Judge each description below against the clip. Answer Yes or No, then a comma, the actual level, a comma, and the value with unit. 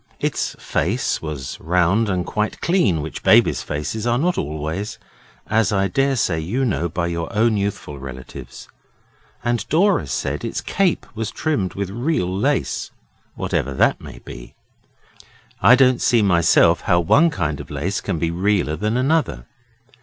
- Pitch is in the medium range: No, low, 100 Hz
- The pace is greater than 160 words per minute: No, average, 155 wpm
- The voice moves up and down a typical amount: No, wide, 6.3 semitones